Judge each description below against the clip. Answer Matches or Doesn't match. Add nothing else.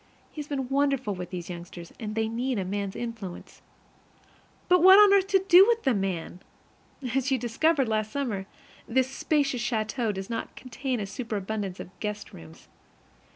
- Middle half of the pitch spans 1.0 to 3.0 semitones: Doesn't match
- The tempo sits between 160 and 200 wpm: Matches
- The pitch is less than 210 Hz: Doesn't match